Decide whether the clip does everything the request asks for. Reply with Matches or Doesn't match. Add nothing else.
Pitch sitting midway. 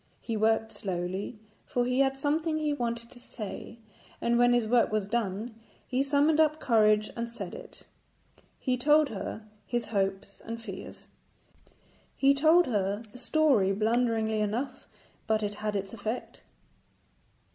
Doesn't match